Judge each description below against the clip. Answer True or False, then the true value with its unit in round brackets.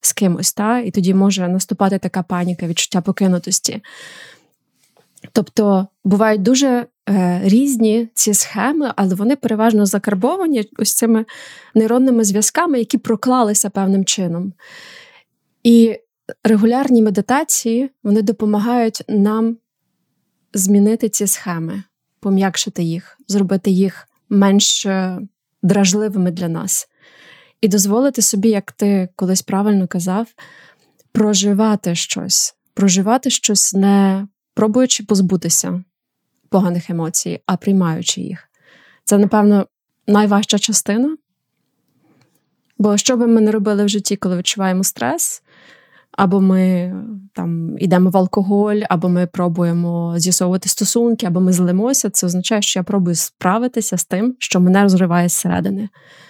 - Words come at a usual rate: True (115 wpm)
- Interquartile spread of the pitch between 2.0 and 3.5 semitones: True (3.1 semitones)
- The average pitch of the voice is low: False (205 Hz)